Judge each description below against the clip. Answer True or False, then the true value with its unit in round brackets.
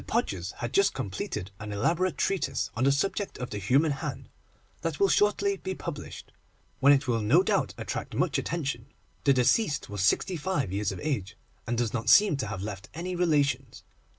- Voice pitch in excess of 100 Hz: True (140 Hz)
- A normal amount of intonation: False (7.8 semitones)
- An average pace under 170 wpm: False (185 wpm)